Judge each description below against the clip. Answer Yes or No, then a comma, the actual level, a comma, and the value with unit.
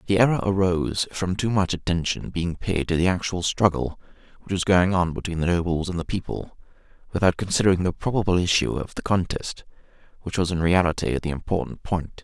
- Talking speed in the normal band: Yes, average, 185 wpm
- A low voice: Yes, very low, 90 Hz